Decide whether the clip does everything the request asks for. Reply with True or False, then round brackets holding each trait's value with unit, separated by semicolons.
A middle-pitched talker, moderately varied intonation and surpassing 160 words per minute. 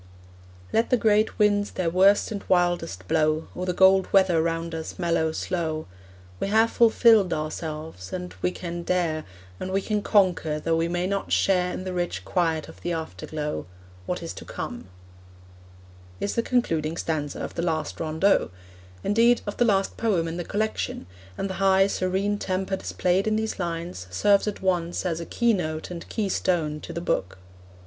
True (180 Hz; 3.4 semitones; 170 wpm)